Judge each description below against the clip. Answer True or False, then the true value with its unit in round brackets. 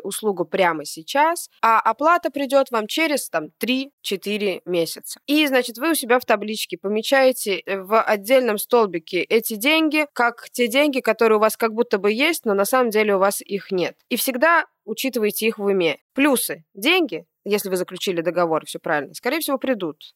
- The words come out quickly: True (175 wpm)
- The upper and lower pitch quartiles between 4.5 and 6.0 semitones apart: True (5.3 semitones)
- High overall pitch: True (220 Hz)